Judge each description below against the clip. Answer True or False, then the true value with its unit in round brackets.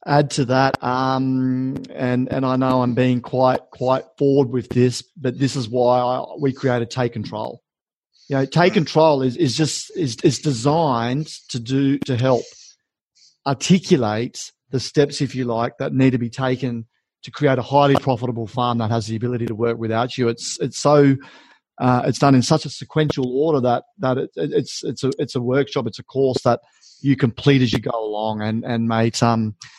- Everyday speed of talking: True (195 wpm)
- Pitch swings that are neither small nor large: False (2.3 semitones)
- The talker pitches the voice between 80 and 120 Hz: False (130 Hz)